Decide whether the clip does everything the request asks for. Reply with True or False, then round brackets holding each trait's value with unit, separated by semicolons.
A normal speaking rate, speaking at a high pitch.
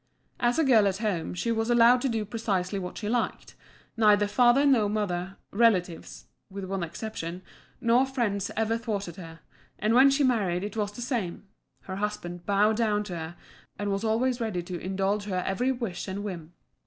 True (185 wpm; 210 Hz)